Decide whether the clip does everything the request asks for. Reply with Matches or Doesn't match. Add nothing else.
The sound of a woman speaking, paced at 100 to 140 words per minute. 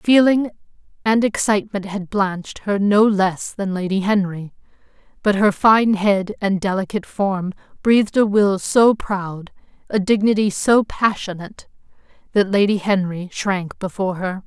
Matches